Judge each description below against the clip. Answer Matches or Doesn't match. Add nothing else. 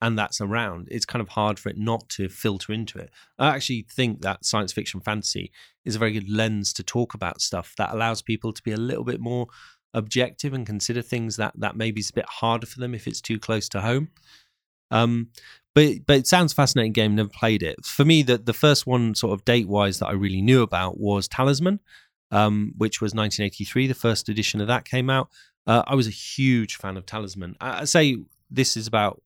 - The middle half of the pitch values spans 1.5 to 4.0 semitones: Matches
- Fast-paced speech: Matches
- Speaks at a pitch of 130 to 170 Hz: Doesn't match